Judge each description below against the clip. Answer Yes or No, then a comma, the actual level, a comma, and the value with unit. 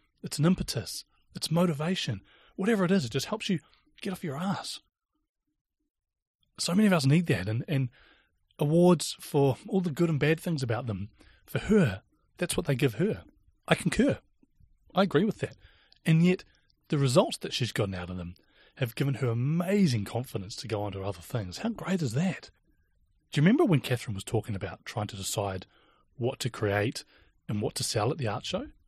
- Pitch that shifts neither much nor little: No, wide, 8.4 semitones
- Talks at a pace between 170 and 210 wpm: Yes, average, 195 wpm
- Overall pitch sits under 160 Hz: Yes, medium, 140 Hz